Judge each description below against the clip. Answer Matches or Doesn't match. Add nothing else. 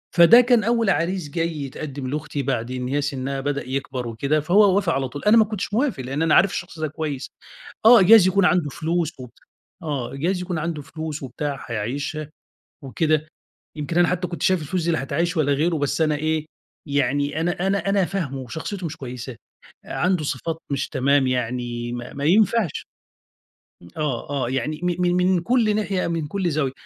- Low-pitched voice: Doesn't match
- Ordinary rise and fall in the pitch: Matches